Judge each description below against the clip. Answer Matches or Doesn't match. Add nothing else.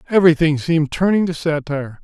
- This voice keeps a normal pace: Matches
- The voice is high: Doesn't match